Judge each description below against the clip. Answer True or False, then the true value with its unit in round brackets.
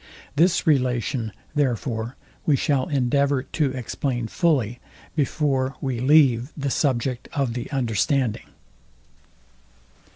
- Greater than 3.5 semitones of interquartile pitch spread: False (2.9 semitones)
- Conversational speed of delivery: False (100 wpm)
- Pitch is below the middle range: True (130 Hz)